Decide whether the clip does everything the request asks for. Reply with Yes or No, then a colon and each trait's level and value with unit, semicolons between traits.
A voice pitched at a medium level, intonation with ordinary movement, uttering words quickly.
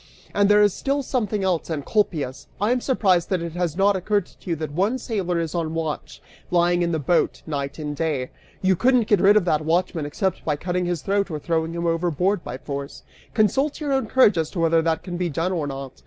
Yes: medium, 175 Hz; average, 4.0 semitones; fast, 230 wpm